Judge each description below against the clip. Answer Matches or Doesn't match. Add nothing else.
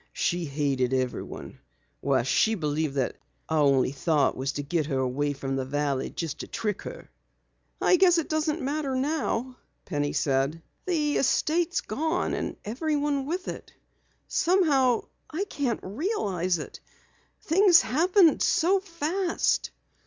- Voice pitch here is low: Doesn't match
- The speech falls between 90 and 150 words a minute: Matches